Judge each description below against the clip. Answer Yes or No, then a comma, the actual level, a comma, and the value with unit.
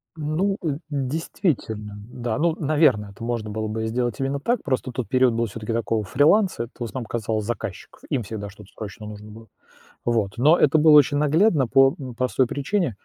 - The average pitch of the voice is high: No, low, 125 Hz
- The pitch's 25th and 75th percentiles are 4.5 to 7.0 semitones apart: Yes, average, 5.0 semitones